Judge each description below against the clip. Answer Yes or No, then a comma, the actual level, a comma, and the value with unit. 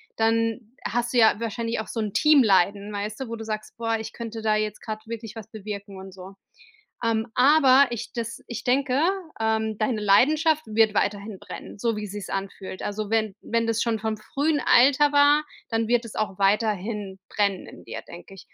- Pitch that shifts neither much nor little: No, narrow, 2.3 semitones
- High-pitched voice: Yes, high, 220 Hz